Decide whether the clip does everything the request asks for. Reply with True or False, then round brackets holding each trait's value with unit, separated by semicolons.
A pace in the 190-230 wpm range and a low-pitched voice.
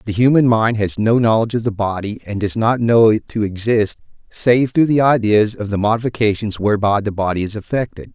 True (205 wpm; 110 Hz)